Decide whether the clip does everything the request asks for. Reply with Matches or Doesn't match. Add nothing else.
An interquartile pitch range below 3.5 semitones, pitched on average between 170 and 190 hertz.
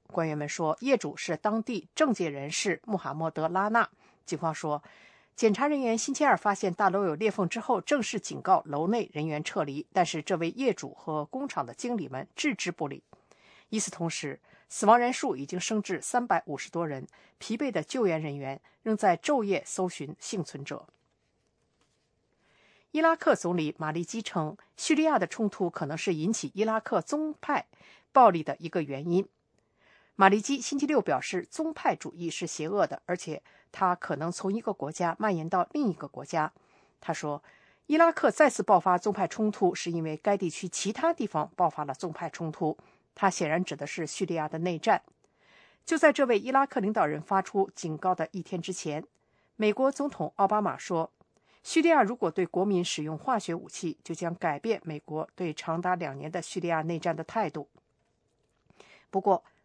Doesn't match